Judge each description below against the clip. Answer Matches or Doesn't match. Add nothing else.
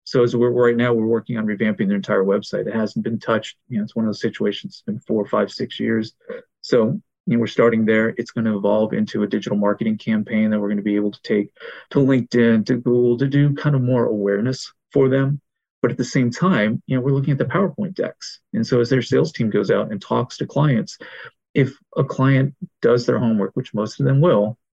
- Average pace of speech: Doesn't match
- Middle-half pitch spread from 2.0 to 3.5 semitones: Doesn't match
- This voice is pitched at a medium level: Doesn't match